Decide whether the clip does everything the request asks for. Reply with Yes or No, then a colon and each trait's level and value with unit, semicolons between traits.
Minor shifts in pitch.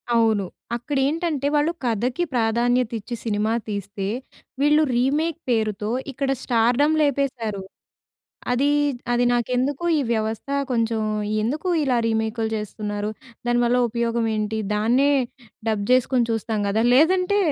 No: average, 3.9 semitones